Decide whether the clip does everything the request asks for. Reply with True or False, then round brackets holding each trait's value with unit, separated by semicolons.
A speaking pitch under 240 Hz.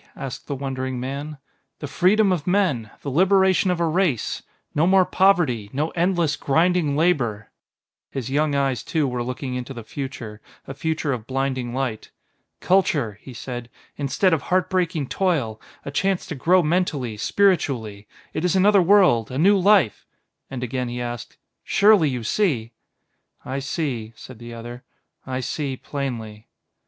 True (140 Hz)